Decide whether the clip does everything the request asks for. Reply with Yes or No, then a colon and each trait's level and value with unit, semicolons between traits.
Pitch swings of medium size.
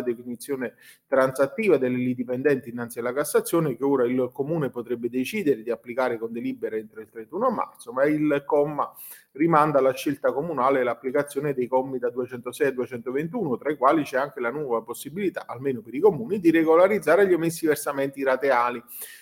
Yes: average, 3.0 semitones